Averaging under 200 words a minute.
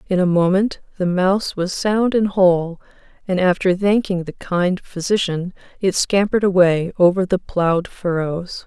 Yes: average, 150 wpm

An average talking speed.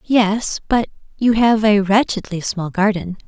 Yes: average, 145 wpm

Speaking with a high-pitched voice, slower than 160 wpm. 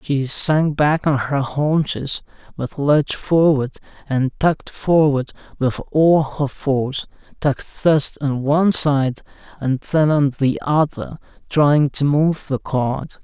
No: medium, 145 Hz; average, 140 wpm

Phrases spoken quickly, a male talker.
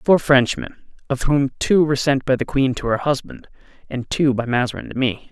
Yes: fast, 225 wpm; male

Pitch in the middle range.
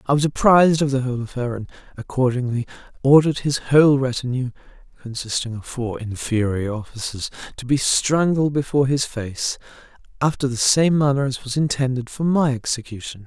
No: low, 130 Hz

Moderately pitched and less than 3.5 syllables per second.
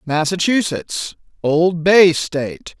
Yes: medium, 170 Hz; 3.3 syllables/s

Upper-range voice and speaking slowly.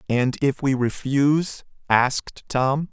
No: low, 135 Hz; slow, 125 wpm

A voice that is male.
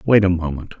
Yes: male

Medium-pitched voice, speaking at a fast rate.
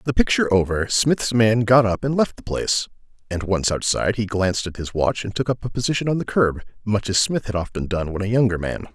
No: low, 110 Hz; fast, 250 wpm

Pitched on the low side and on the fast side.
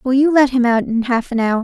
No: very high, 250 Hz; fast, 330 wpm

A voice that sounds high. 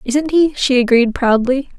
Yes: very high, 260 Hz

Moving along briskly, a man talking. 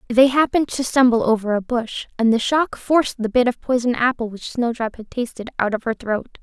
No: fast, 225 wpm; female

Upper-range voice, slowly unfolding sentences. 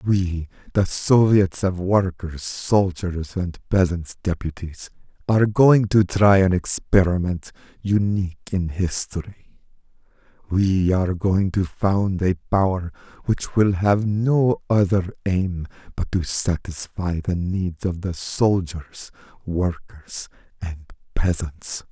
No: very low, 95 Hz; slow, 115 wpm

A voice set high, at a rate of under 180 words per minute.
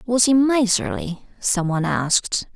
Yes: high, 215 Hz; average, 140 wpm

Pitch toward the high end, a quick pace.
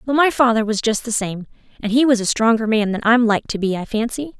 Yes: high, 230 Hz; fast, 275 wpm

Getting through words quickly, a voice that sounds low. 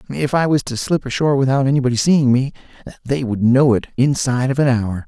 Yes: fast, 215 wpm; low, 130 Hz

